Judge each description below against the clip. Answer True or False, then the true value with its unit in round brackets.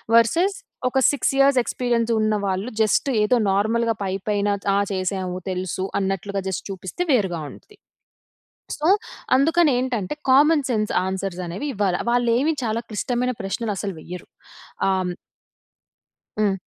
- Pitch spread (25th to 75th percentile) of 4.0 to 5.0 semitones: True (4.7 semitones)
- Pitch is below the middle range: False (215 Hz)